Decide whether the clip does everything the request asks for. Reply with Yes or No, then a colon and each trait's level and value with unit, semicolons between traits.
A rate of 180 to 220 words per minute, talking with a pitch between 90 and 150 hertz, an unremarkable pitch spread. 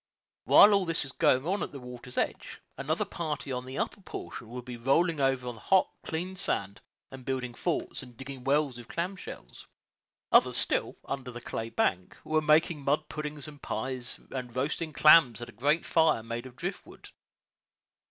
Yes: average, 190 wpm; low, 135 Hz; average, 4.2 semitones